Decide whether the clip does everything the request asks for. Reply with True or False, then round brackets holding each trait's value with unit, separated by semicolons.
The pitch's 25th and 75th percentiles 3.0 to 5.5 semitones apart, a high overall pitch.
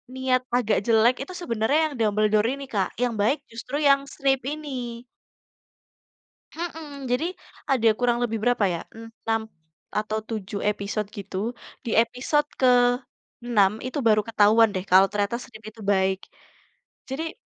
True (3.3 semitones; 225 Hz)